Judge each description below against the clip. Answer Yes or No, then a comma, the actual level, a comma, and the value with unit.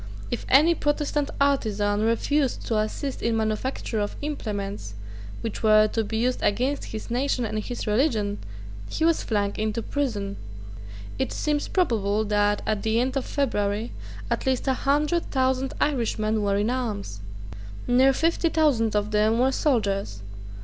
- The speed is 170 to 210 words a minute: No, average, 155 wpm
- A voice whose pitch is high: Yes, high, 230 Hz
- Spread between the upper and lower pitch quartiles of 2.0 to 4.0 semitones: No, average, 4.4 semitones